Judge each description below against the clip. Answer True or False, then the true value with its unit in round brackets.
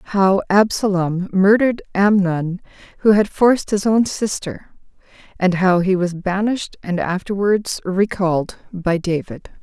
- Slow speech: True (125 wpm)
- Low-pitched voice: False (190 Hz)